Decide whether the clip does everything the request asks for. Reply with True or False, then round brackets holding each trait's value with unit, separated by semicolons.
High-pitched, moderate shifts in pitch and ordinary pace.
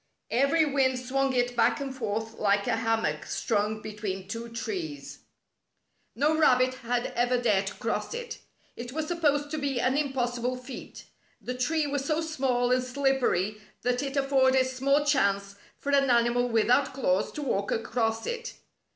True (255 Hz; 3.5 semitones; 160 wpm)